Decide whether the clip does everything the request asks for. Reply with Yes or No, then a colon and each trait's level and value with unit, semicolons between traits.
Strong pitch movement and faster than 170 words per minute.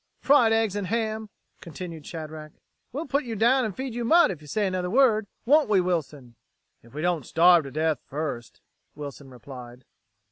Yes: wide, 6.9 semitones; average, 180 wpm